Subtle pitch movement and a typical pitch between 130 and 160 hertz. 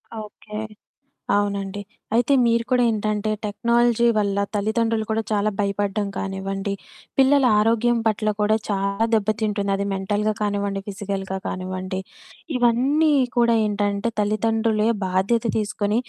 No: narrow, 2.3 semitones; high, 210 Hz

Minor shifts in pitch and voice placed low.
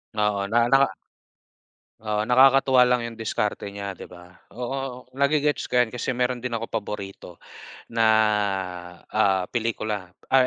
No: average, 3.4 semitones; low, 115 Hz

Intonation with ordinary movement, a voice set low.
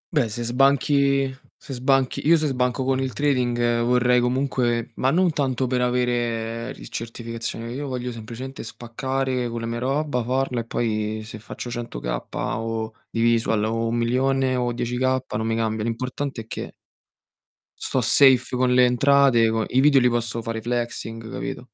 No: narrow, 2.3 semitones; low, 125 Hz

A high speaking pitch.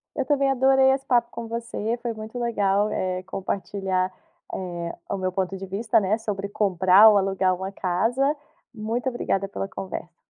Yes: high, 200 Hz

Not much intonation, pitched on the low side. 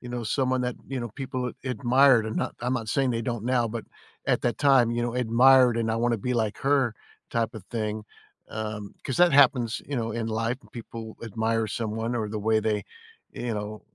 Yes: narrow, 2.2 semitones; low, 115 Hz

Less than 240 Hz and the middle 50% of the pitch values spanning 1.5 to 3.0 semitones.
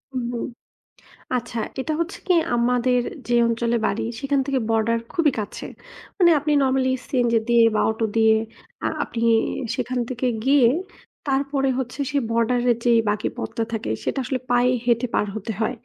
No: high, 245 Hz; narrow, 2.6 semitones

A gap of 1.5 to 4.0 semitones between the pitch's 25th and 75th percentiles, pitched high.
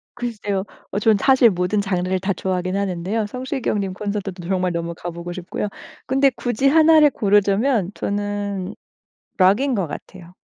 Yes: average, 3.5 semitones; high, 200 Hz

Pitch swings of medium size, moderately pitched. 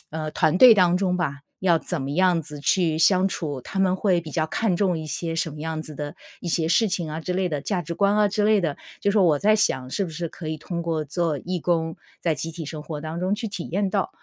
Yes: average, 3.2 semitones; medium, 170 Hz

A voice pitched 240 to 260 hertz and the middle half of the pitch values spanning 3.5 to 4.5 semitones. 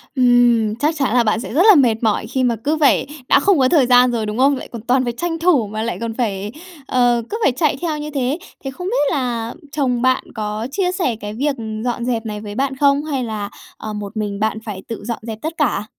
Yes: high, 245 Hz; average, 4.2 semitones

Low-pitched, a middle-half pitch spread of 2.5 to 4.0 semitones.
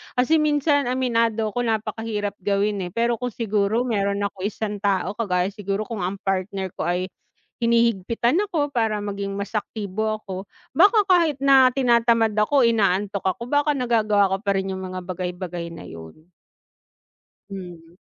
No: high, 210 Hz; average, 3.6 semitones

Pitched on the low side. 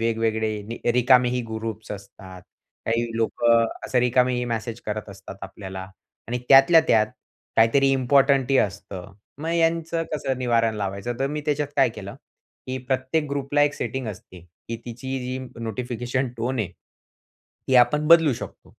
Yes: low, 120 Hz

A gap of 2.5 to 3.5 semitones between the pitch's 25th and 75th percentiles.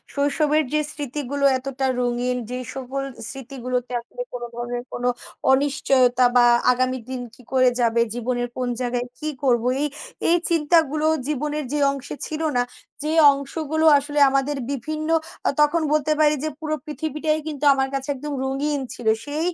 Yes: average, 3.2 semitones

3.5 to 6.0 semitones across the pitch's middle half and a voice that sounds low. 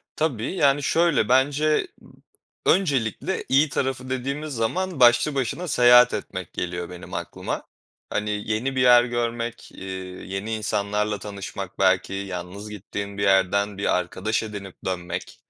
Yes: average, 5.1 semitones; low, 110 Hz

